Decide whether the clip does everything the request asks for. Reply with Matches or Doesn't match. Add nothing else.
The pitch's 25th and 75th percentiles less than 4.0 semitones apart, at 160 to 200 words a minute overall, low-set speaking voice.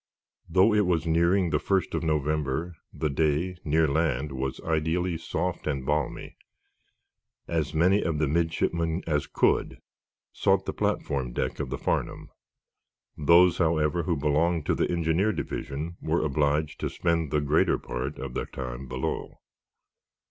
Doesn't match